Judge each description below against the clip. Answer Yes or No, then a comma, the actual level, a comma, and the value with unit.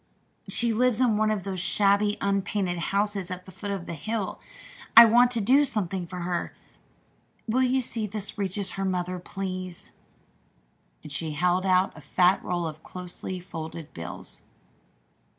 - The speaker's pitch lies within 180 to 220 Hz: Yes, high, 190 Hz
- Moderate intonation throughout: Yes, average, 3.0 semitones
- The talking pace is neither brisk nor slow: Yes, average, 165 wpm